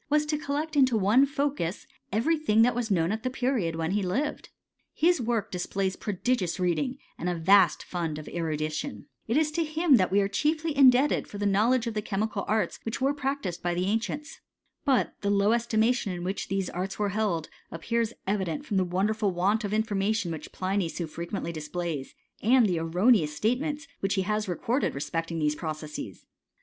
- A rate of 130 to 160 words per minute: No, average, 170 wpm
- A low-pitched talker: No, high, 205 Hz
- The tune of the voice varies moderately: No, wide, 6.0 semitones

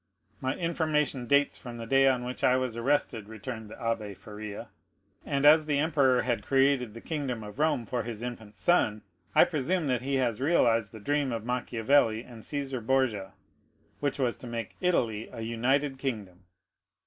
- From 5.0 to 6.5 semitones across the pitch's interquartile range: No, average, 3.8 semitones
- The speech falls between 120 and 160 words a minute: No, average, 175 wpm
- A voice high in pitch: No, low, 125 Hz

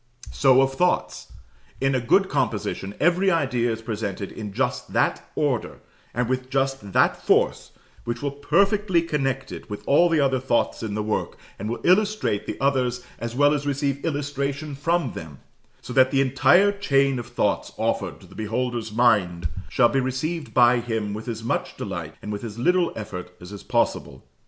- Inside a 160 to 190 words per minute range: Yes, average, 180 wpm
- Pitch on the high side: No, low, 130 Hz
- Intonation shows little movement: No, average, 4.2 semitones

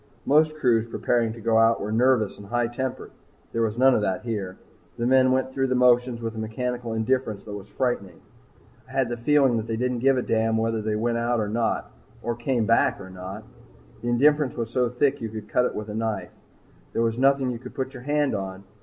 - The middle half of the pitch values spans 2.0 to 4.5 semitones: Yes, narrow, 2.6 semitones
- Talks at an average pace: No, fast, 230 wpm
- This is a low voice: Yes, low, 115 Hz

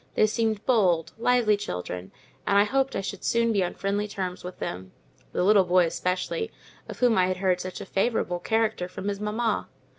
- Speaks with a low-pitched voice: No, high, 200 Hz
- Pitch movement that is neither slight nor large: Yes, average, 3.5 semitones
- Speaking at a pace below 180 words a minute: No, average, 190 wpm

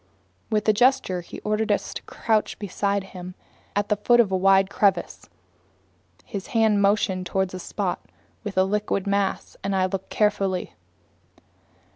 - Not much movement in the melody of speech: Yes, narrow, 1.8 semitones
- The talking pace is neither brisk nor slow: Yes, average, 155 wpm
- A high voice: Yes, high, 200 Hz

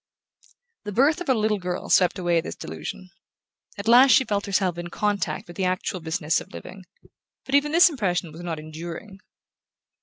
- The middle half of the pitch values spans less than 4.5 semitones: Yes, average, 4.1 semitones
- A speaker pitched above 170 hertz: Yes, high, 190 Hz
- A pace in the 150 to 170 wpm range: No, average, 180 wpm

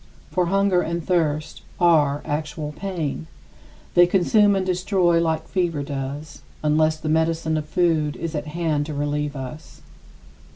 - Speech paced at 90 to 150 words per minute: Yes, average, 140 wpm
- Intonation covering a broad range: No, average, 2.8 semitones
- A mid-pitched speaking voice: Yes, medium, 160 Hz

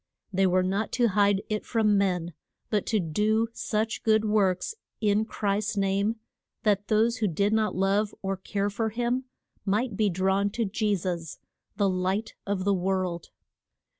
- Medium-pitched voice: No, high, 205 Hz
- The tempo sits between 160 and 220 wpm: Yes, average, 165 wpm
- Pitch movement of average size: No, narrow, 2.1 semitones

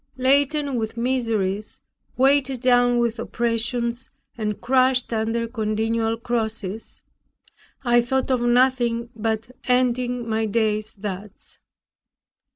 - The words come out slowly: Yes, slow, 100 wpm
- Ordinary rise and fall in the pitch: No, narrow, 2.2 semitones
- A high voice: Yes, high, 235 Hz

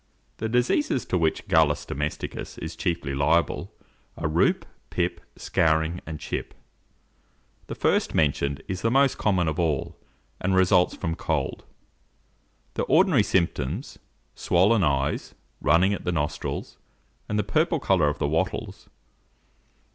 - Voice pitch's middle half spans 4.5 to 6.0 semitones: Yes, average, 4.8 semitones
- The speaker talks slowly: Yes, slow, 130 wpm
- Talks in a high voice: No, very low, 85 Hz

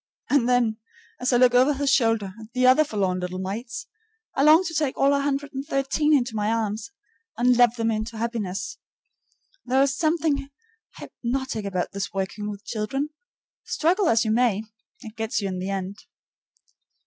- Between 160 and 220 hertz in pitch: No, high, 240 Hz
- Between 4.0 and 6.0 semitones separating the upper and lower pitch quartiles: Yes, average, 4.4 semitones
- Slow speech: No, average, 165 wpm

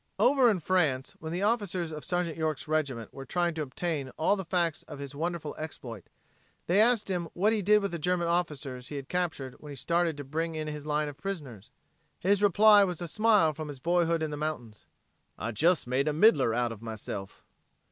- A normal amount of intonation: Yes, average, 4.1 semitones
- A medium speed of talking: No, fast, 210 wpm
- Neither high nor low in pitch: Yes, medium, 160 Hz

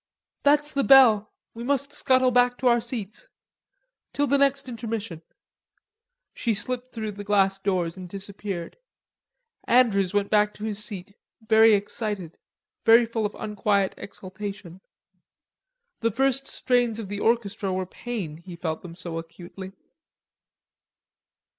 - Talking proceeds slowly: Yes, slow, 130 wpm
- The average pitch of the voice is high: Yes, high, 210 Hz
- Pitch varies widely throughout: No, average, 4.0 semitones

